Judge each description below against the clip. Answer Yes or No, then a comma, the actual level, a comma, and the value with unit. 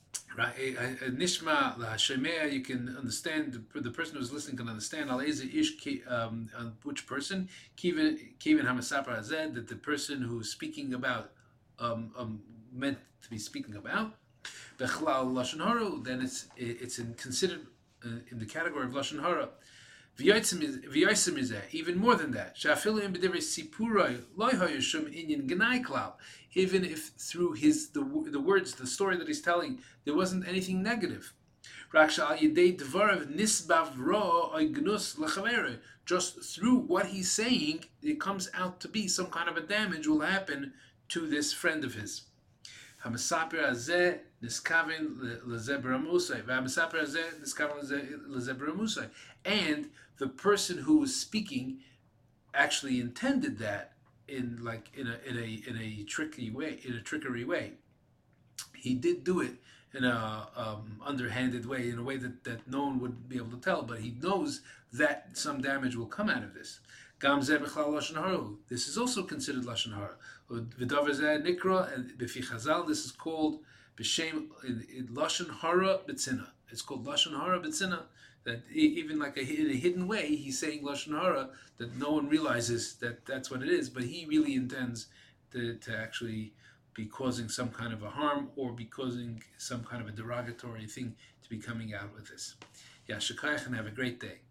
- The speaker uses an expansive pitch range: Yes, wide, 7.5 semitones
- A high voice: No, medium, 140 Hz